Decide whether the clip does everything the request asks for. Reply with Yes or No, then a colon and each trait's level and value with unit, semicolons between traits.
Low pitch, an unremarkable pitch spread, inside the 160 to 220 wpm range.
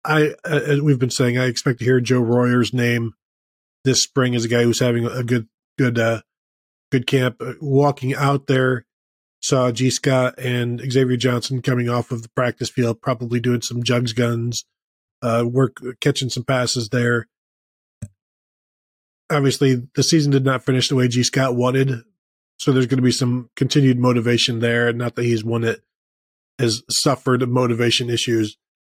No: low, 125 Hz; narrow, 1.8 semitones; average, 165 wpm